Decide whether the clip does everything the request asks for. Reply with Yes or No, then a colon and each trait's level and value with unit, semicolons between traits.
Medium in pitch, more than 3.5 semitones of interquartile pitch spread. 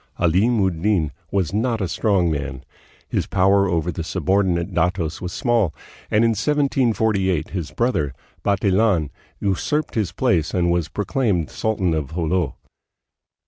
No: very low, 95 Hz; average, 4.2 semitones